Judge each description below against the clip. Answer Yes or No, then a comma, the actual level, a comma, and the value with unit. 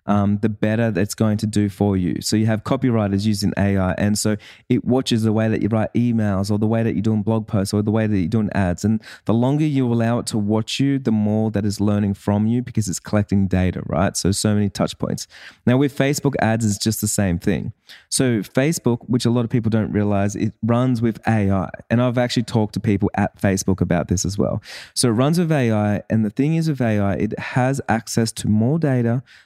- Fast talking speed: Yes, fast, 240 wpm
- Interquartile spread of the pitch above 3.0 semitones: No, average, 2.7 semitones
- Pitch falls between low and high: No, low, 110 Hz